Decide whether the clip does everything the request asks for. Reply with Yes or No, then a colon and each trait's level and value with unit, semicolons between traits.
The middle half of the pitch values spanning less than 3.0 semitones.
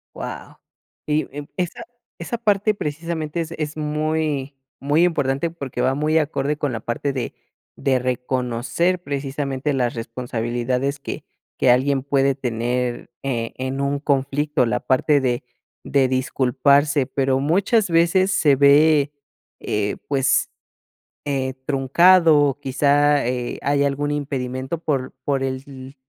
Yes: narrow, 2.6 semitones